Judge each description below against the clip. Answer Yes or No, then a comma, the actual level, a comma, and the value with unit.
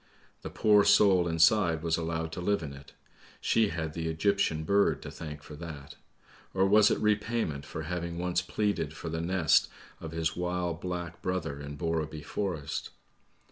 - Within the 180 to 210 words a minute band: No, average, 170 wpm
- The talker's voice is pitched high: No, very low, 85 Hz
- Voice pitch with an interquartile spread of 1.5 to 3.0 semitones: Yes, average, 2.7 semitones